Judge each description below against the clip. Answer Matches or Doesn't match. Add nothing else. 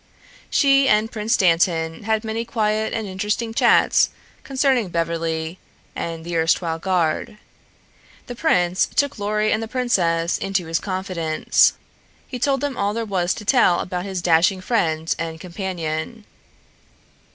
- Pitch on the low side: Doesn't match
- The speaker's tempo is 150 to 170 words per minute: Doesn't match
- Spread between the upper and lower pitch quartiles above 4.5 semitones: Matches